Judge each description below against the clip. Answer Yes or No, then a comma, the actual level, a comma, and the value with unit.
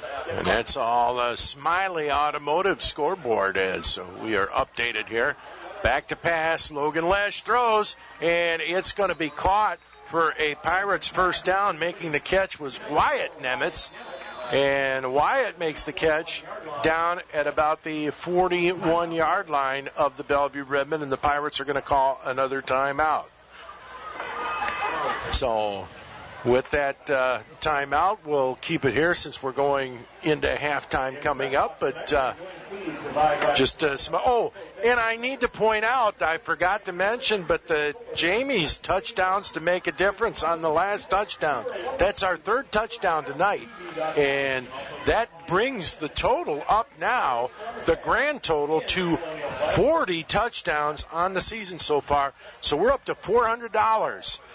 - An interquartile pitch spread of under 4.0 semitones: No, average, 4.7 semitones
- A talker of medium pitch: Yes, medium, 160 Hz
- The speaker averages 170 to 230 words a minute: No, average, 145 wpm